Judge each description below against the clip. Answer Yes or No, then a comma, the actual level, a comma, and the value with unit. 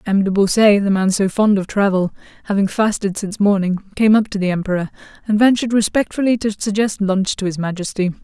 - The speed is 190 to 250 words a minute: Yes, average, 195 wpm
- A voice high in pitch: Yes, high, 200 Hz